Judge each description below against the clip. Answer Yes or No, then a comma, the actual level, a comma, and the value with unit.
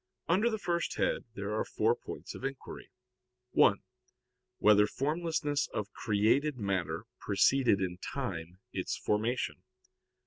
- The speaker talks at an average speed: No, slow, 125 wpm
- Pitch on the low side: Yes, low, 115 Hz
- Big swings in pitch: Yes, wide, 6.5 semitones